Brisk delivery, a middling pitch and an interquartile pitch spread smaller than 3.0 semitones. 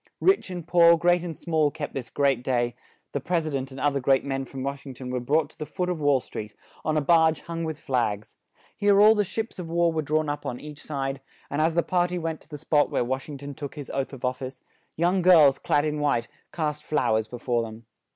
No: fast, 260 wpm; medium, 145 Hz; average, 3.7 semitones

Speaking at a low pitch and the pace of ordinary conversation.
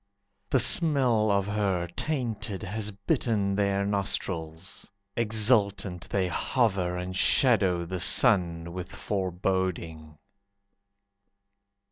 No: low, 100 Hz; slow, 90 wpm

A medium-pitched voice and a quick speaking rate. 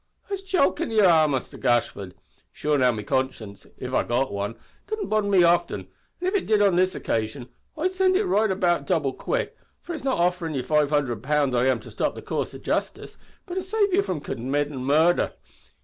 Yes: medium, 165 Hz; fast, 215 wpm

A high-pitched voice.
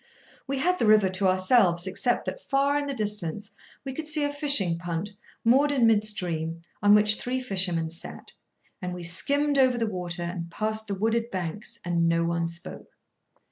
Yes: high, 205 Hz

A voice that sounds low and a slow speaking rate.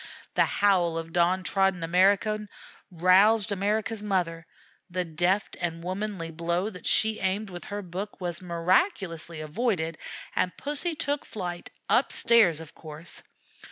No: medium, 185 Hz; slow, 130 wpm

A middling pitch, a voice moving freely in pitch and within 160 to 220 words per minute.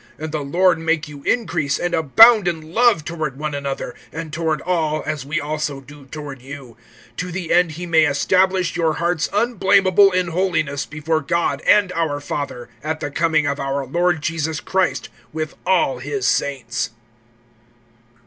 No: medium, 160 Hz; average, 3.5 semitones; average, 165 wpm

